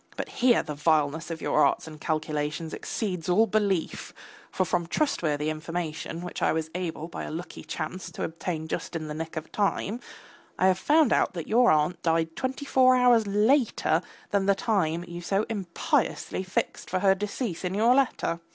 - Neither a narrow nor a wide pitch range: Yes, average, 4.5 semitones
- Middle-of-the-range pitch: Yes, medium, 175 Hz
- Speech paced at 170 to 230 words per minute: Yes, average, 185 wpm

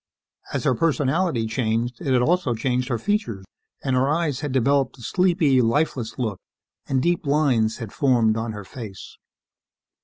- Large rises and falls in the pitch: No, average, 4.3 semitones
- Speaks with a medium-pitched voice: No, low, 130 Hz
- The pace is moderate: Yes, average, 160 wpm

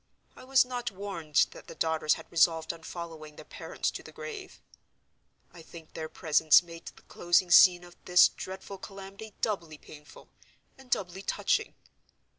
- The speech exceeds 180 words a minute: No, average, 160 wpm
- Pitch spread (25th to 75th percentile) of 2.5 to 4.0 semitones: Yes, average, 3.6 semitones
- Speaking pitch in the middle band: Yes, medium, 175 Hz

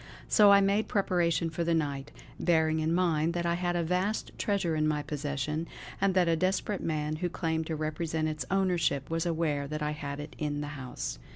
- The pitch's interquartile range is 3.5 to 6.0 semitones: No, narrow, 2.6 semitones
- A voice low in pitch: No, medium, 160 Hz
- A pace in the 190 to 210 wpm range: Yes, fast, 205 wpm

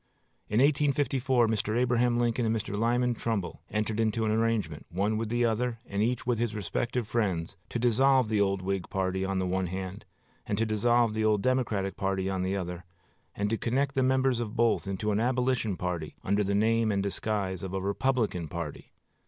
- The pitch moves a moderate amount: Yes, average, 3.7 semitones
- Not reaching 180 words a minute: No, average, 195 wpm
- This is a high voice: No, low, 110 Hz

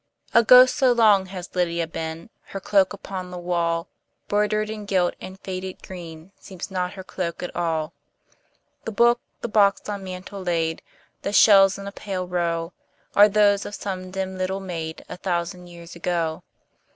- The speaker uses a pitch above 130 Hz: Yes, medium, 185 Hz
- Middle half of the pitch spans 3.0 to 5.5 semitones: No, narrow, 2.6 semitones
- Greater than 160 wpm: Yes, average, 170 wpm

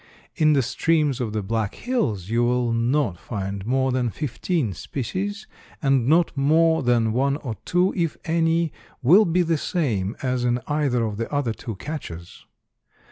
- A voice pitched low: Yes, low, 130 Hz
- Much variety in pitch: Yes, wide, 5.8 semitones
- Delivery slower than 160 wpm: No, average, 165 wpm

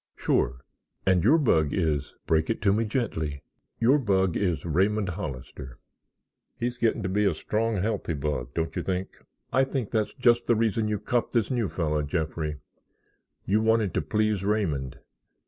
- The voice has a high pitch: No, low, 100 Hz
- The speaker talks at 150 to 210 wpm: Yes, average, 165 wpm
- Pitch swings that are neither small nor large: No, wide, 6.0 semitones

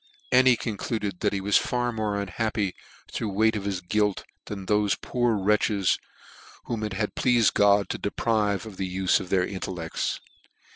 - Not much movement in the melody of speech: Yes, narrow, 2.2 semitones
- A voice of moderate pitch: No, low, 105 Hz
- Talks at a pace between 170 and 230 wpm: Yes, average, 180 wpm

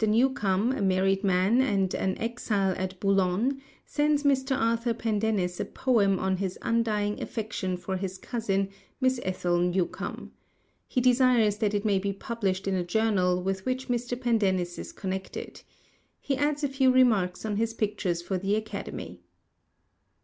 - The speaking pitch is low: No, high, 205 Hz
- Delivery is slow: No, average, 155 wpm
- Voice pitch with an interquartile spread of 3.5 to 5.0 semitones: Yes, average, 4.1 semitones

